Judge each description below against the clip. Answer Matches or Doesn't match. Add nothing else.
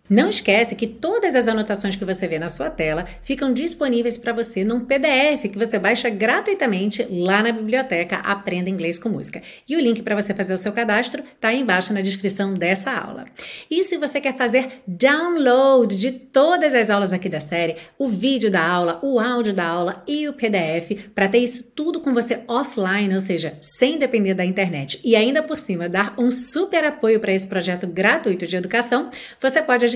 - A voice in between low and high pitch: Doesn't match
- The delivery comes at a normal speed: Doesn't match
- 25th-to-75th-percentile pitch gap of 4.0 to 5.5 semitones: Matches